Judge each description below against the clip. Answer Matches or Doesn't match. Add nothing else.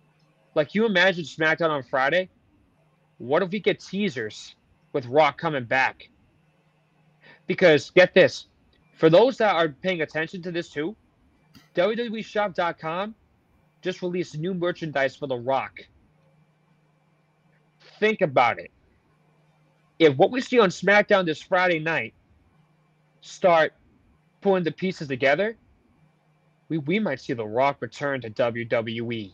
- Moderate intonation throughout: Matches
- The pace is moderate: Doesn't match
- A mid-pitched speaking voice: Matches